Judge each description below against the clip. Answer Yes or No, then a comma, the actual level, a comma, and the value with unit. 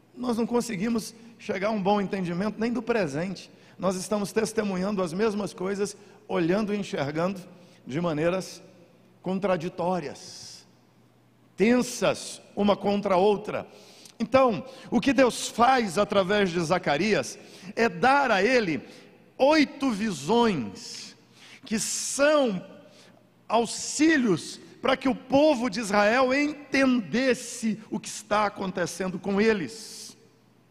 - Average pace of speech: No, slow, 115 wpm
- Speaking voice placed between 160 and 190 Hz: No, high, 210 Hz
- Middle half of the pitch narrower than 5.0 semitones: Yes, average, 4.1 semitones